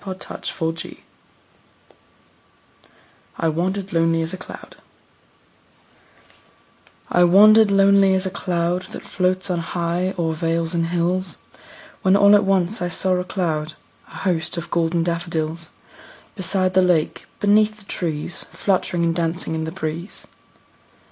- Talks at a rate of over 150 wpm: No, slow, 135 wpm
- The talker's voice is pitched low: No, medium, 175 Hz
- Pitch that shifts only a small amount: Yes, narrow, 2.3 semitones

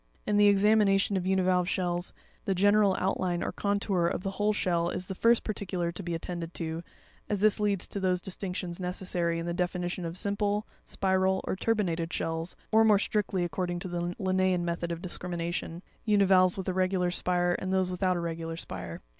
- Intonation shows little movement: Yes, narrow, 2.1 semitones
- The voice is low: No, medium, 185 Hz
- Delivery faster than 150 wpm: Yes, average, 190 wpm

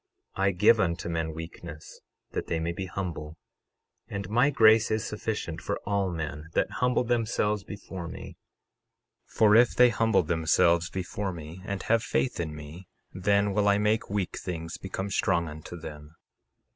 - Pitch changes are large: No, average, 4.2 semitones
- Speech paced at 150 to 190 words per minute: Yes, average, 160 wpm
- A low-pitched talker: Yes, very low, 95 Hz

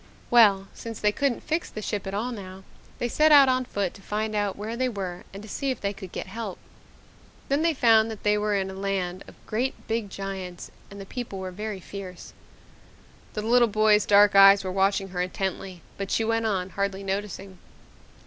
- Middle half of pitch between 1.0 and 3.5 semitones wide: Yes, average, 2.7 semitones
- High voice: Yes, high, 205 Hz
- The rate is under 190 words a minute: No, fast, 205 wpm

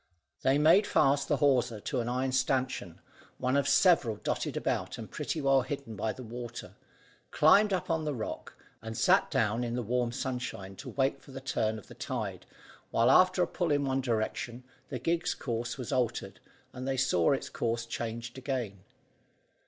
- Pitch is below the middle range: Yes, low, 130 Hz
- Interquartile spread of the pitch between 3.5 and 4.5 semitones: No, average, 3.1 semitones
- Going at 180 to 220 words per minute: Yes, average, 185 wpm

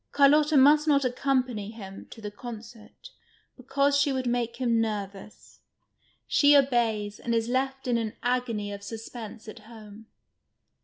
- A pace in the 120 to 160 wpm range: Yes, average, 145 wpm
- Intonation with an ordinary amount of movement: Yes, average, 3.7 semitones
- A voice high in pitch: Yes, high, 235 Hz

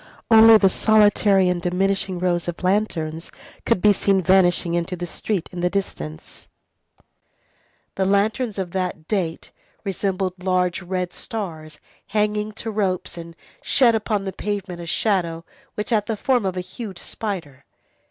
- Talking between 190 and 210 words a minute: No, average, 150 wpm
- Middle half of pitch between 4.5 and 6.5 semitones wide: No, average, 3.0 semitones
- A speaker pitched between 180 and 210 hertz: Yes, high, 190 Hz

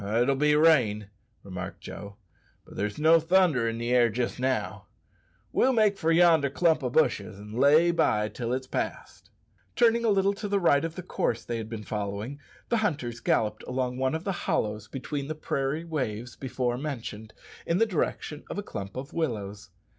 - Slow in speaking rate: No, average, 185 wpm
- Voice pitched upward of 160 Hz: No, low, 130 Hz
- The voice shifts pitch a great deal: Yes, wide, 6.8 semitones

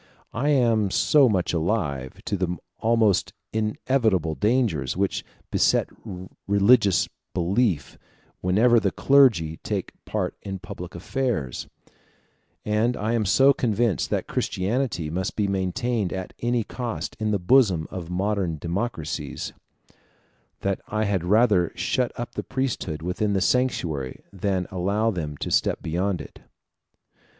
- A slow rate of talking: Yes, slow, 130 wpm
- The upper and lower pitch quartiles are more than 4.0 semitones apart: Yes, average, 4.8 semitones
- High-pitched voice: No, low, 100 Hz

